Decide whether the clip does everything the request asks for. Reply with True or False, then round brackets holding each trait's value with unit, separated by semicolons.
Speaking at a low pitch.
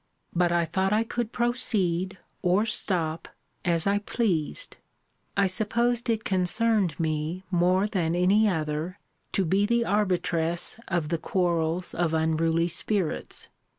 False (180 Hz)